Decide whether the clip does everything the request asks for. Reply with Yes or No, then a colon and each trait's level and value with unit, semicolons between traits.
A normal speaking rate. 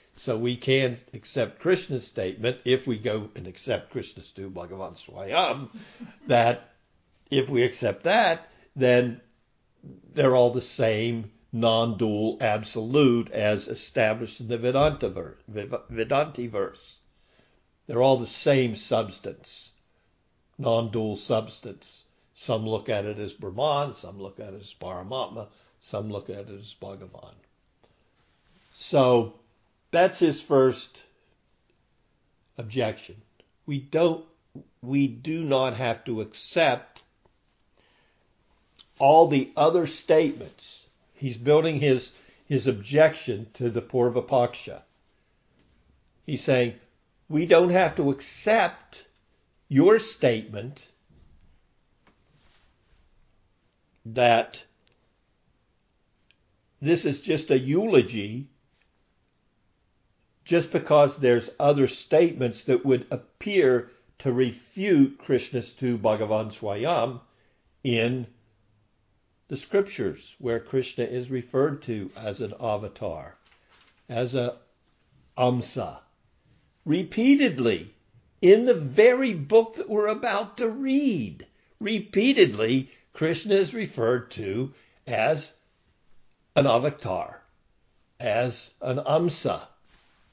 No: slow, 100 wpm